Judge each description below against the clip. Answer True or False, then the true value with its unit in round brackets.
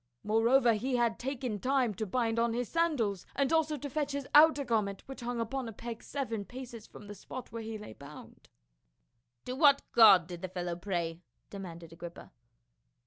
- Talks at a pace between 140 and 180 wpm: False (190 wpm)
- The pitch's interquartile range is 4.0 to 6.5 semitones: True (4.8 semitones)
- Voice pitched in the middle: False (230 Hz)